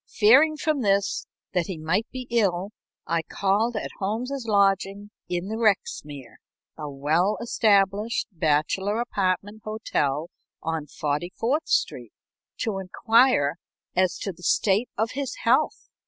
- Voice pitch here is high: Yes, high, 200 Hz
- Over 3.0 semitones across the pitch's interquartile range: Yes, average, 4.5 semitones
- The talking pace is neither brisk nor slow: No, slow, 130 wpm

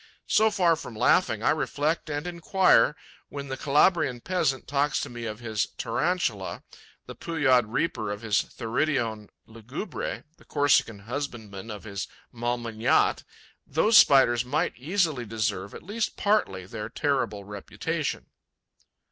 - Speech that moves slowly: Yes, slow, 130 wpm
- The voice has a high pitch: No, low, 125 Hz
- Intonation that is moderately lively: No, wide, 5.9 semitones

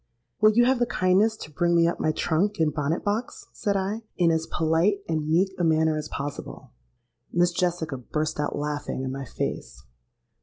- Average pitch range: Yes, average, 4.1 semitones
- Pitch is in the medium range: Yes, medium, 165 Hz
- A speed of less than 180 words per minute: No, average, 185 wpm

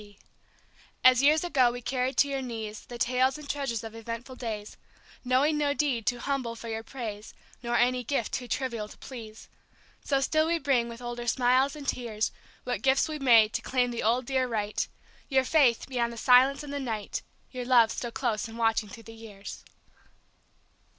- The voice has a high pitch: Yes, high, 245 Hz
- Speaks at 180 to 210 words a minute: Yes, average, 190 wpm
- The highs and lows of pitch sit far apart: No, average, 2.8 semitones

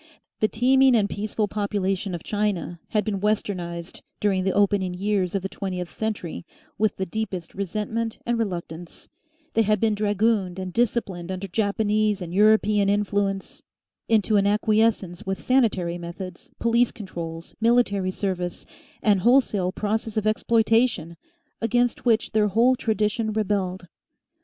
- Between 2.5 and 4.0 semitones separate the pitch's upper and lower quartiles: Yes, average, 2.8 semitones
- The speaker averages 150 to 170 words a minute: No, average, 140 wpm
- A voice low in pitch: No, high, 205 Hz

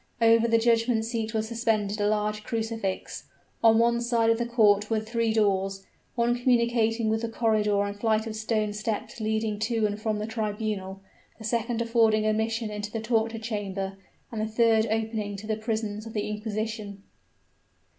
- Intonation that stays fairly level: Yes, narrow, 1.3 semitones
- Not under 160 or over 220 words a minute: Yes, average, 175 wpm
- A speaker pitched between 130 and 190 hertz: No, high, 220 Hz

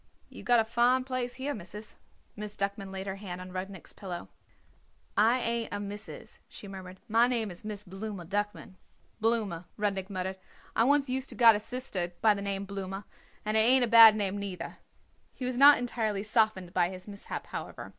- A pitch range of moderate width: Yes, average, 3.3 semitones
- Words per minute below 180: No, average, 190 wpm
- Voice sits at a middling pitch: No, high, 205 Hz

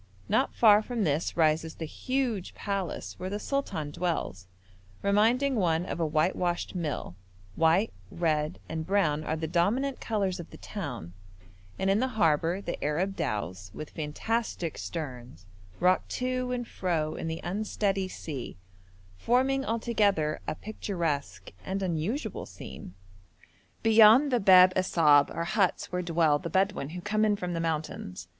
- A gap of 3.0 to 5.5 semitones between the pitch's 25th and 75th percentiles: Yes, average, 5.2 semitones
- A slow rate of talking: No, average, 145 wpm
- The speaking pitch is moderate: Yes, medium, 180 Hz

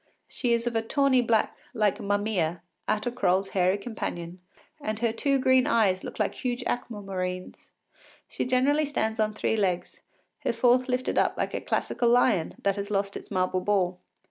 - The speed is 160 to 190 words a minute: Yes, average, 175 wpm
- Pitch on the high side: Yes, high, 215 Hz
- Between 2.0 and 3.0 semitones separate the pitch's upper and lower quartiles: No, average, 4.1 semitones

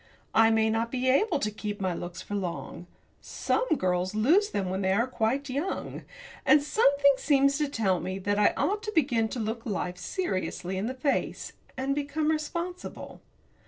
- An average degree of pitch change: No, wide, 6.3 semitones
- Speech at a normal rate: Yes, average, 180 wpm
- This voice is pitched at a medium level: No, high, 235 Hz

